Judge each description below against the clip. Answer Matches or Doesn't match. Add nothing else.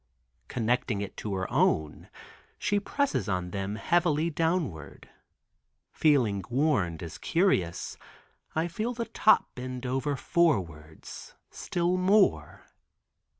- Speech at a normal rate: Doesn't match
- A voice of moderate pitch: Doesn't match